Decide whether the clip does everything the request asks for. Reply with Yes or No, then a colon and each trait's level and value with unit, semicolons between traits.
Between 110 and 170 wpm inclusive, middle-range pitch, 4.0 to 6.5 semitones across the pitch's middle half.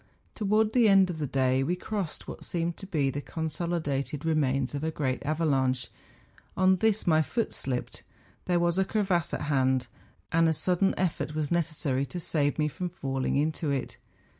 No: average, 185 wpm; medium, 160 Hz; average, 4.3 semitones